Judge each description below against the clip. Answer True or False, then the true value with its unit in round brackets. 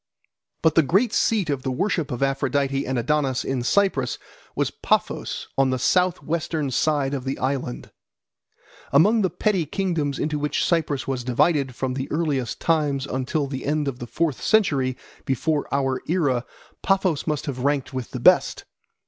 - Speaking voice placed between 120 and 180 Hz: True (140 Hz)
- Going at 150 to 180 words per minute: True (165 wpm)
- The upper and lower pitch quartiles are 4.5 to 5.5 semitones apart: False (3.5 semitones)